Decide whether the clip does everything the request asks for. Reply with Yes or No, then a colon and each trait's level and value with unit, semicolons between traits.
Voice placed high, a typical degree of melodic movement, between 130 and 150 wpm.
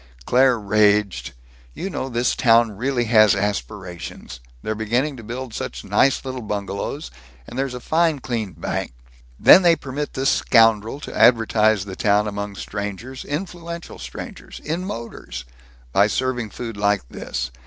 No: low, 115 Hz; average, 4.2 semitones; average, 145 wpm